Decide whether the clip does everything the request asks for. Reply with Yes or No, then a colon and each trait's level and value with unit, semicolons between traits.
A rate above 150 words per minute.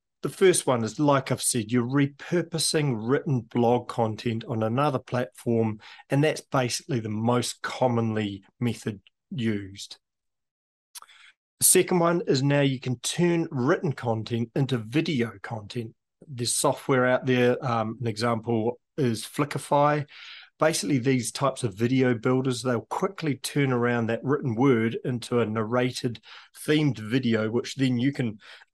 No: average, 140 wpm